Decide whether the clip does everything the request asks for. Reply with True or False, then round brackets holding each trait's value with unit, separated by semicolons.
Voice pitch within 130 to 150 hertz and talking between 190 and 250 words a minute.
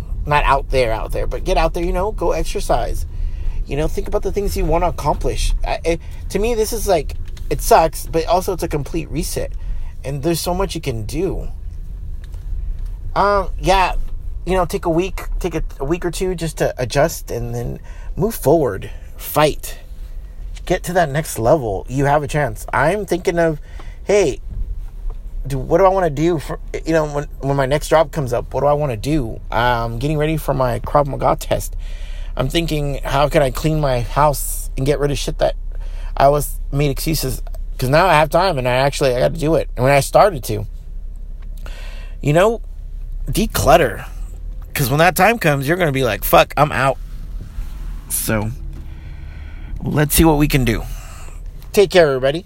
True (135 Hz; 195 wpm)